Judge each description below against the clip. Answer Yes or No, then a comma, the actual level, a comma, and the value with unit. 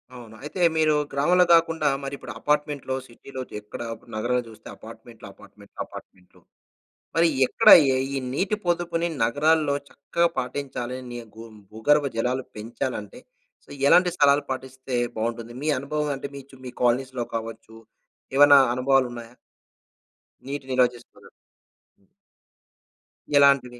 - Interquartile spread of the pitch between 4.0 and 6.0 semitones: No, average, 3.5 semitones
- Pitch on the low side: Yes, low, 130 Hz